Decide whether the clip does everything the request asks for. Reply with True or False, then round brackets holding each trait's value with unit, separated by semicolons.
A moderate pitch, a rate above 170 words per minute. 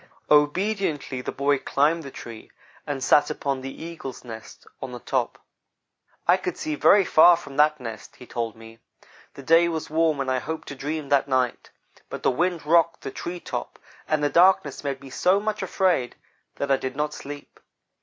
True (145 Hz; 190 wpm)